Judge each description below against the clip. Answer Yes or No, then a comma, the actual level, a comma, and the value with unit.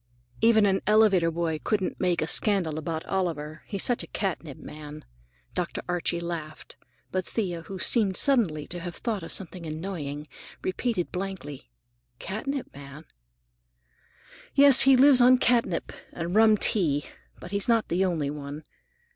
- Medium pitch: Yes, medium, 180 Hz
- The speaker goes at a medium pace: Yes, average, 145 wpm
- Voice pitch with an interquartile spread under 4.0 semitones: No, average, 5.2 semitones